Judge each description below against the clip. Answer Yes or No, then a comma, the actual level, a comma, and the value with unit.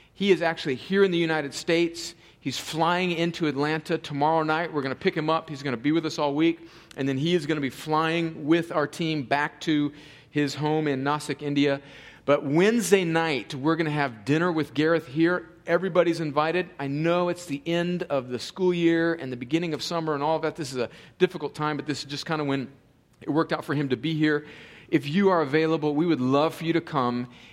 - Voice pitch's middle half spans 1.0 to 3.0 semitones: Yes, narrow, 2.5 semitones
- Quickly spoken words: Yes, fast, 235 wpm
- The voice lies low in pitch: No, medium, 155 Hz